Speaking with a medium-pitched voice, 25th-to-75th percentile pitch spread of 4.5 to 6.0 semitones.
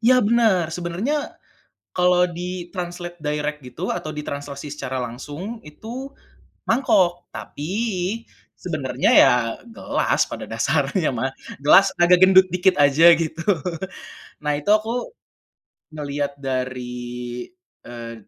Yes: medium, 175 Hz; average, 4.9 semitones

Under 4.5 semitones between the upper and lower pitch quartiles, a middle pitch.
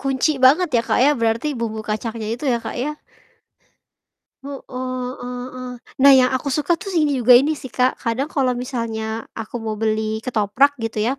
No: average, 3.3 semitones; very high, 250 Hz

